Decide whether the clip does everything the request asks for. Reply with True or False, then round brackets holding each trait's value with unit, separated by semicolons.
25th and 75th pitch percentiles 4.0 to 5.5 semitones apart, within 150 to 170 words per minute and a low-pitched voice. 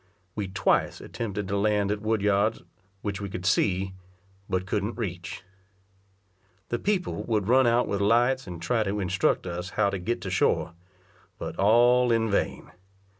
False (3.2 semitones; 165 wpm; 100 Hz)